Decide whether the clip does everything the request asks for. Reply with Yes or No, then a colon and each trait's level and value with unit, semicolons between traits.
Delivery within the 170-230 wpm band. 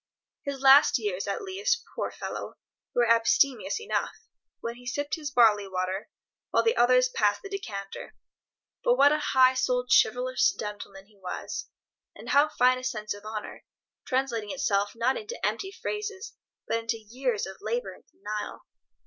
No: average, 160 wpm